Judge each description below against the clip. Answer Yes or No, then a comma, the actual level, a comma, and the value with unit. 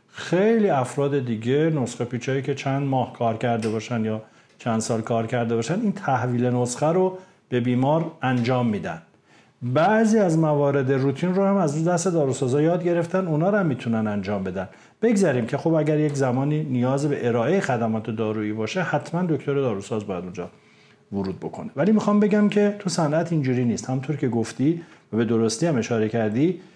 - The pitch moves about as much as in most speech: No, wide, 6.0 semitones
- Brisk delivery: Yes, fast, 175 wpm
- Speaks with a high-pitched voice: No, low, 135 Hz